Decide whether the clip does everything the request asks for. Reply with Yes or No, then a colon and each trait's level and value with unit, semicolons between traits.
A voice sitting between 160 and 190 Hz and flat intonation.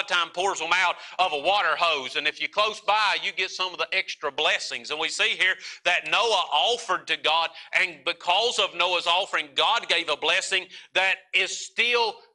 No: medium, 185 Hz; average, 3.3 semitones